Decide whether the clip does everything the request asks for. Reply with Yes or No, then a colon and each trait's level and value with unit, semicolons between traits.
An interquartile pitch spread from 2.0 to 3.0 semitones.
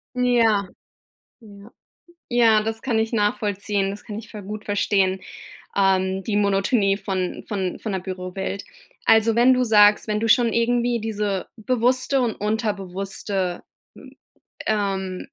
Yes: narrow, 2.5 semitones